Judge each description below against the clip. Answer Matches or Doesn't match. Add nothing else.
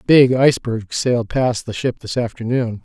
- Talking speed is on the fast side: Doesn't match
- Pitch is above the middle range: Doesn't match